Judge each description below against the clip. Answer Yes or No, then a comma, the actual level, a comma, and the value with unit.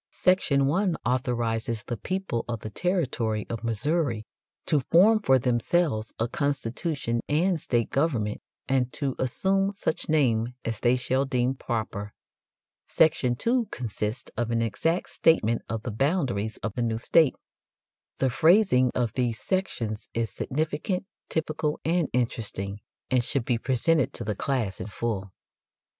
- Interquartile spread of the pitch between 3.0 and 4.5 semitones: No, wide, 5.6 semitones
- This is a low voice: Yes, low, 125 Hz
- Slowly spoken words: No, average, 145 wpm